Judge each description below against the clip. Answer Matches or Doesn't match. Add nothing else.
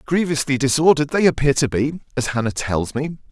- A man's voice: Matches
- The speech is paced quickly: Doesn't match